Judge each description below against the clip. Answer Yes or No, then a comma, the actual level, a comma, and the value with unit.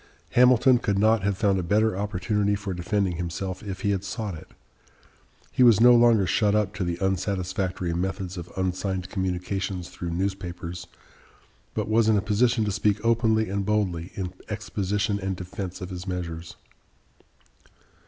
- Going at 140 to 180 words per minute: Yes, average, 160 wpm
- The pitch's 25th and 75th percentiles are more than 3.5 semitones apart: No, narrow, 2.6 semitones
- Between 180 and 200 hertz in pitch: No, very low, 95 Hz